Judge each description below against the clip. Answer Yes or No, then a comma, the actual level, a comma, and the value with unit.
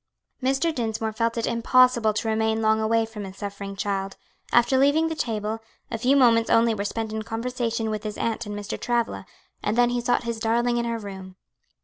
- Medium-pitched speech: No, high, 225 Hz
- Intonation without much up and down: Yes, narrow, 1.8 semitones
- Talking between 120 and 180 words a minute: No, fast, 205 wpm